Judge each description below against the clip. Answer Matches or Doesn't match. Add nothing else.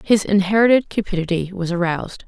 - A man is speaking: Doesn't match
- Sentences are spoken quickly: Doesn't match